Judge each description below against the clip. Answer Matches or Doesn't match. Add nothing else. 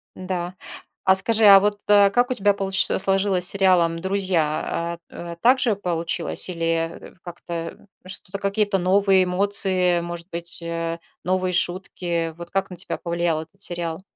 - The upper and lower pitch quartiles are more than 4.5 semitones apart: Doesn't match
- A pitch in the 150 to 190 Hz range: Matches